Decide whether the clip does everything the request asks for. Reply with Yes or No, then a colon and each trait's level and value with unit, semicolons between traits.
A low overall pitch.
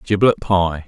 Yes: very low, 95 Hz